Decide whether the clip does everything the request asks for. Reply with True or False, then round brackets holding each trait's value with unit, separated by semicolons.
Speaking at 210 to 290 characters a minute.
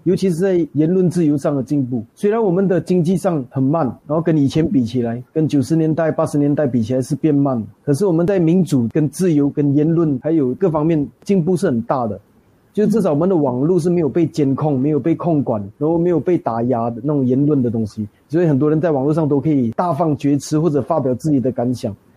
False (345 characters per minute)